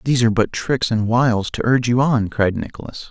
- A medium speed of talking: No, fast, 230 wpm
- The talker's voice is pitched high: No, low, 120 Hz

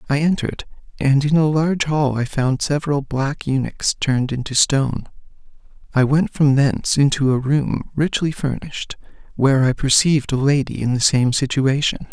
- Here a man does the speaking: Yes, male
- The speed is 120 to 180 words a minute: Yes, average, 165 wpm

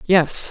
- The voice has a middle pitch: Yes, medium, 175 Hz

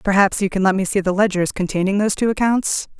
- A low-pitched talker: No, high, 195 Hz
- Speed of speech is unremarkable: No, fast, 240 wpm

